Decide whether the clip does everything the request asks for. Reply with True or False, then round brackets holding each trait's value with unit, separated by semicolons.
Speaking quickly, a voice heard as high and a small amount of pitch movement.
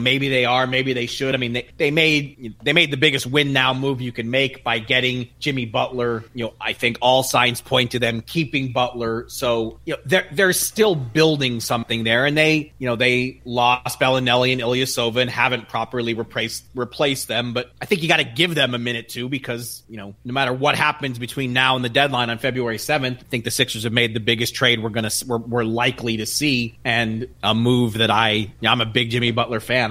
False (230 wpm; 125 Hz; 2.2 semitones)